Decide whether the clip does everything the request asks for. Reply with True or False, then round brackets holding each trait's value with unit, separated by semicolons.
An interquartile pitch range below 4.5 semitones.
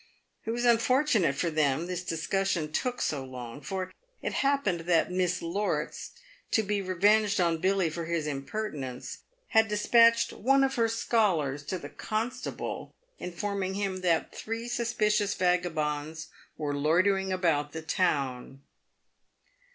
False (5.3 semitones)